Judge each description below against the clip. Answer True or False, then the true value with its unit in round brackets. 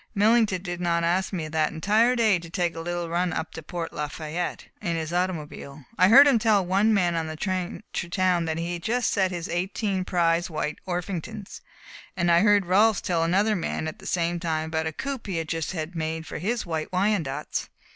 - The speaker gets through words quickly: True (215 wpm)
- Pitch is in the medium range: True (175 Hz)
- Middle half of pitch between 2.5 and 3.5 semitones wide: True (3.1 semitones)